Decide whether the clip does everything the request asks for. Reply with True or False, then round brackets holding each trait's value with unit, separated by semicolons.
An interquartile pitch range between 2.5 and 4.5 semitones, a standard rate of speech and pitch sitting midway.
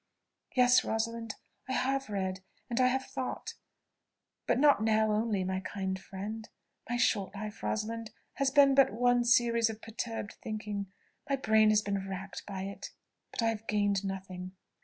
False (3.3 semitones; 160 wpm; 220 Hz)